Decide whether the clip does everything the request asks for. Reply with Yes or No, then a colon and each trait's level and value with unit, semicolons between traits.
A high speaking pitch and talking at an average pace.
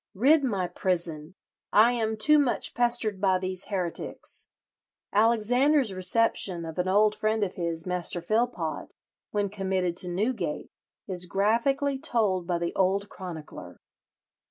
No: high, 195 Hz; slow, 130 wpm